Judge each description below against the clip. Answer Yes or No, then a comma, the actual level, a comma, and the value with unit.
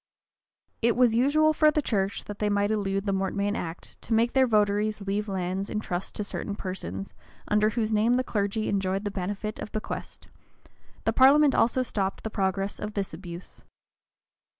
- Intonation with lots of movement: No, narrow, 2.6 semitones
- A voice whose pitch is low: No, high, 205 Hz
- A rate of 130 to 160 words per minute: No, average, 185 wpm